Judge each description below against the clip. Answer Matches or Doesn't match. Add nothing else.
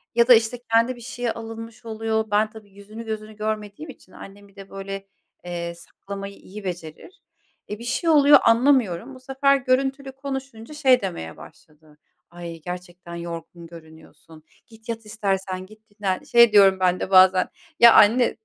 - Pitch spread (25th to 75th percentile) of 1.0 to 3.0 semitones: Doesn't match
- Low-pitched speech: Doesn't match